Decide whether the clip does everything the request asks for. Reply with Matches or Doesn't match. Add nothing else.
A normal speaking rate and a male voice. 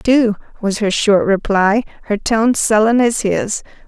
Doesn't match